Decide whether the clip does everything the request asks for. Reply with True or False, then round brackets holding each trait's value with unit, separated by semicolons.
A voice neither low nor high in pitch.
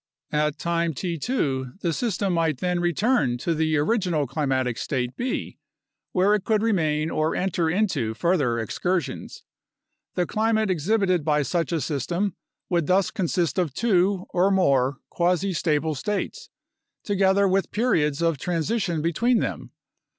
True (170 Hz)